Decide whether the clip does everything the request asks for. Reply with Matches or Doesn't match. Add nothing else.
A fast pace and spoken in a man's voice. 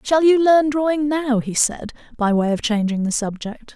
Doesn't match